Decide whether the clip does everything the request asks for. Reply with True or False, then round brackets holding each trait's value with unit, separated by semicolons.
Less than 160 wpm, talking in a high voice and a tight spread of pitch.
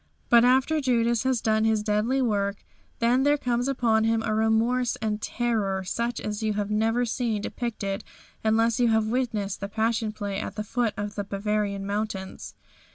False (175 wpm; 220 Hz; 2.3 semitones)